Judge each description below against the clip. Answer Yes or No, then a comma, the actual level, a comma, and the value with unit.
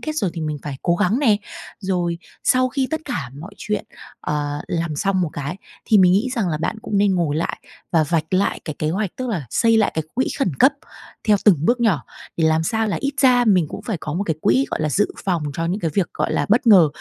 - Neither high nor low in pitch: Yes, medium, 180 Hz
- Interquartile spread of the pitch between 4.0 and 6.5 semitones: Yes, wide, 5.4 semitones